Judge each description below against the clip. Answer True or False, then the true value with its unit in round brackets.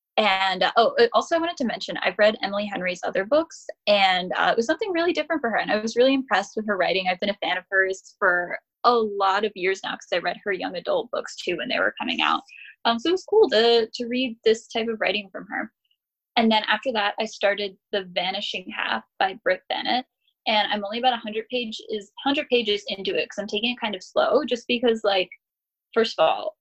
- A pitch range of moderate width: True (3.6 semitones)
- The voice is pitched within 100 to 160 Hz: False (220 Hz)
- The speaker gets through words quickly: True (235 wpm)